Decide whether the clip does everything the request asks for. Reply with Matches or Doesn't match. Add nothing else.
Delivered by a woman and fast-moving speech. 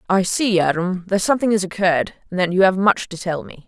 Matches